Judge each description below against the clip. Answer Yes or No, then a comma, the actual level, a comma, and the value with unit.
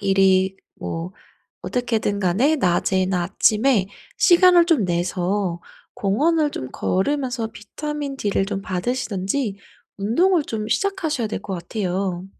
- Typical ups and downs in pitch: No, wide, 6.6 semitones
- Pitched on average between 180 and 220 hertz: Yes, high, 205 Hz